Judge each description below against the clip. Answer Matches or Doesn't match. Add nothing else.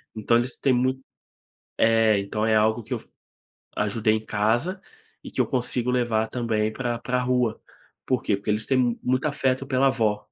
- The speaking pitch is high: Doesn't match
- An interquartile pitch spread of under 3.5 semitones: Matches